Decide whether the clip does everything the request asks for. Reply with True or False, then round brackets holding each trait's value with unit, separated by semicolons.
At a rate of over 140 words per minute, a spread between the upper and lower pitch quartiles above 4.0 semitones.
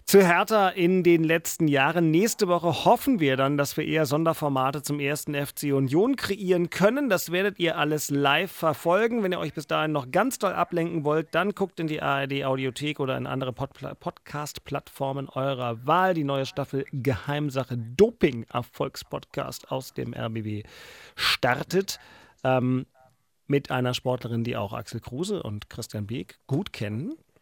True (155 wpm; 4.9 semitones)